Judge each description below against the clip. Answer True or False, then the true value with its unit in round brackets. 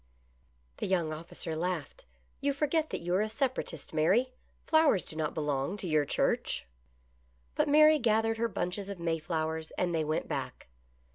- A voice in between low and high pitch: True (180 Hz)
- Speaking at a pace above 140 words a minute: True (165 wpm)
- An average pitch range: False (6.4 semitones)